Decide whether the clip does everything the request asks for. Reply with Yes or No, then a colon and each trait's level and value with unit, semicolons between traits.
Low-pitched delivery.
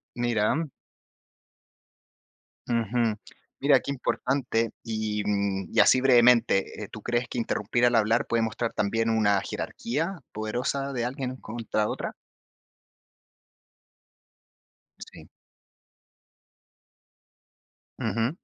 Yes: low, 115 Hz